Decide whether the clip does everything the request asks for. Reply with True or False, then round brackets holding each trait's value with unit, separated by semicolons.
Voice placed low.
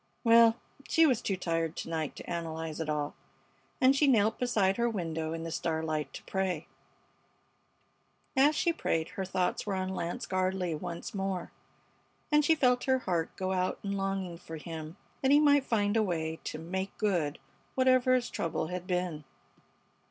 False (185 Hz)